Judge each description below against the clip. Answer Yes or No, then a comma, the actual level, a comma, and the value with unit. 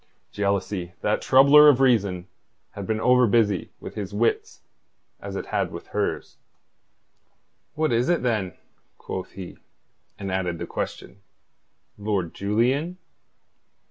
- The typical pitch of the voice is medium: No, low, 105 Hz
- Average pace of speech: No, slow, 125 wpm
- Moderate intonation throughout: Yes, average, 4.8 semitones